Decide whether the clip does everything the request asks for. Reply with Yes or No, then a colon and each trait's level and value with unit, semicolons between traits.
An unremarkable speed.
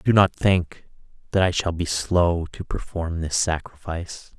Yes: average, 165 wpm